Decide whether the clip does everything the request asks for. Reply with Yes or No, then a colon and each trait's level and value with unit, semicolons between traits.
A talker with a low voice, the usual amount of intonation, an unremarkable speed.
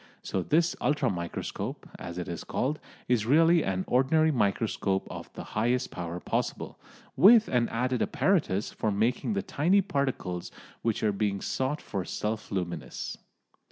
No: low, 120 Hz; wide, 7.3 semitones; average, 150 wpm